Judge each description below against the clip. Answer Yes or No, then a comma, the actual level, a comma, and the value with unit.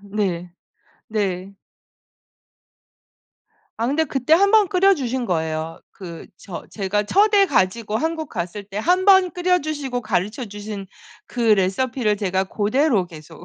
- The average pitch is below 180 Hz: No, high, 215 Hz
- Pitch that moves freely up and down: Yes, wide, 8.4 semitones